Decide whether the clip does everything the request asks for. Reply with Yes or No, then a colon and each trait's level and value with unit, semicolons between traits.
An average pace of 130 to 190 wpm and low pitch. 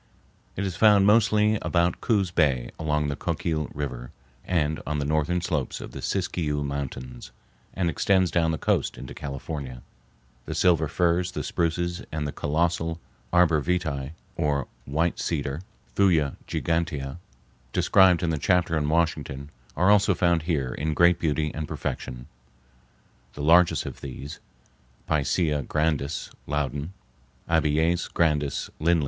Yes: slow, 135 wpm; very low, 80 Hz